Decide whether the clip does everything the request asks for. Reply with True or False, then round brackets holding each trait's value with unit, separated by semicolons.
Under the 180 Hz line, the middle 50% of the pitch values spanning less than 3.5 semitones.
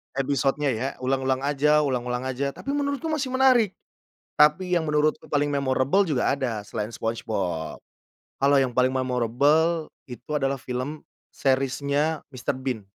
True (135 Hz; 3.0 semitones)